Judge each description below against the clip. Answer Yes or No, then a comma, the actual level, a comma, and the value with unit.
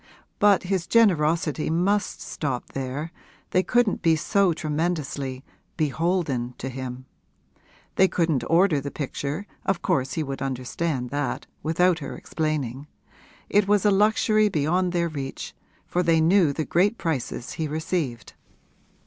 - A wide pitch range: No, average, 4.8 semitones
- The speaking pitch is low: No, medium, 160 Hz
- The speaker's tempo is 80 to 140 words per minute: Yes, slow, 135 wpm